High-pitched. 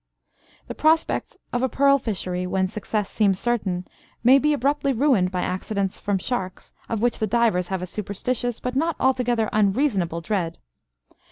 Yes: high, 215 Hz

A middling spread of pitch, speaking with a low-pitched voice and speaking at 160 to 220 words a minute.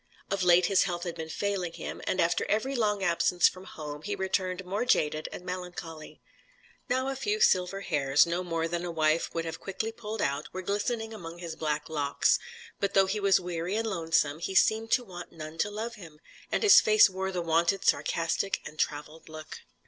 No: average, 3.7 semitones; medium, 180 Hz; average, 200 wpm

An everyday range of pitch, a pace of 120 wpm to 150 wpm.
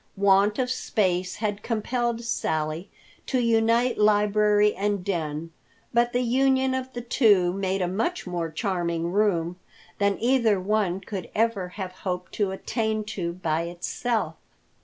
Yes: average, 4.1 semitones; average, 140 wpm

